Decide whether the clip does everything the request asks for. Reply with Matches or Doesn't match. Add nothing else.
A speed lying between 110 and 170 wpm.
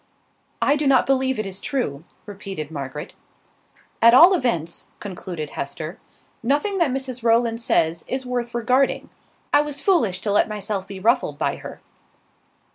Matches